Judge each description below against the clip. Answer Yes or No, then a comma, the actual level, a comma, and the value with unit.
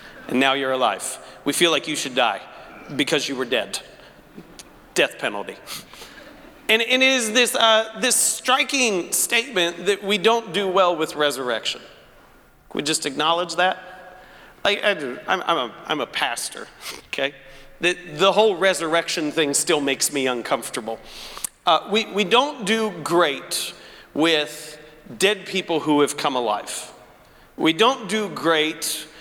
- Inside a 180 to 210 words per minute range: No, average, 145 wpm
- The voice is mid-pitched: Yes, medium, 180 Hz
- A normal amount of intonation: No, wide, 6.2 semitones